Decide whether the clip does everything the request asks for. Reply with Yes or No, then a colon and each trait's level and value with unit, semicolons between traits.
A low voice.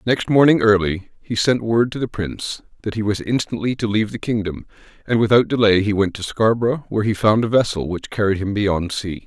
Yes: low, 105 Hz